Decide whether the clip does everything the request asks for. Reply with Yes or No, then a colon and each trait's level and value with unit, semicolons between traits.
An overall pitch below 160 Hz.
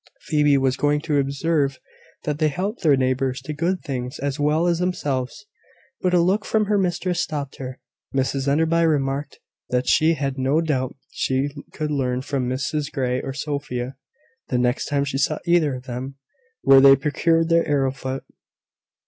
Yes: medium, 140 Hz